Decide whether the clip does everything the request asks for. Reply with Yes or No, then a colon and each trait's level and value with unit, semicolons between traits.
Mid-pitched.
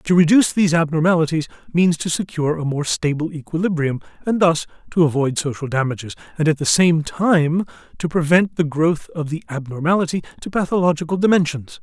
Yes: medium, 160 Hz